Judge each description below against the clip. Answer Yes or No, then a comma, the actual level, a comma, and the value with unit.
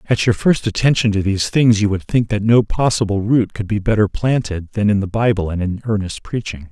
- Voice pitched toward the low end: Yes, low, 105 Hz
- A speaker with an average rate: No, fast, 230 wpm